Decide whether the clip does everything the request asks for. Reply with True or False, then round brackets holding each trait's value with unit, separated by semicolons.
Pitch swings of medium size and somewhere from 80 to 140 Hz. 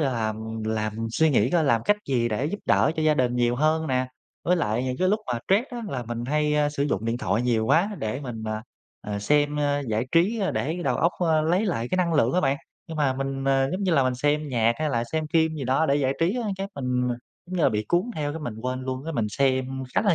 True (4.9 semitones; 135 Hz)